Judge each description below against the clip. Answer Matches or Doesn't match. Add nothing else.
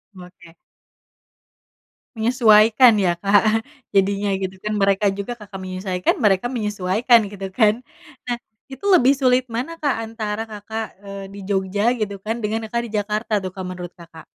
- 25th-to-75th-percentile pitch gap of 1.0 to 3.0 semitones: Matches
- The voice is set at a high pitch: Matches